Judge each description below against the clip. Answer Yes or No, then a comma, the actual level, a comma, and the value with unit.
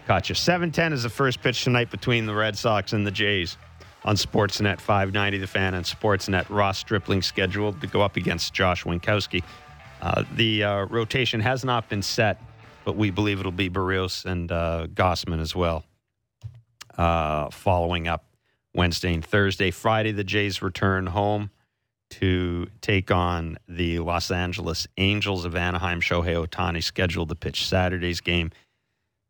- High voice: No, very low, 95 Hz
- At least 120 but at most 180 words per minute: Yes, average, 155 wpm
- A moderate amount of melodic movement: Yes, average, 3.4 semitones